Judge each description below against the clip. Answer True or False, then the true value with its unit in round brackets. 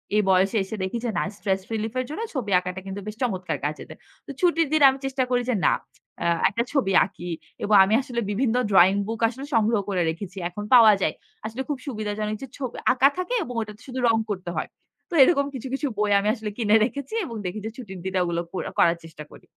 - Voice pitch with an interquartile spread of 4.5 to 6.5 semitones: True (4.9 semitones)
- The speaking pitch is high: True (215 Hz)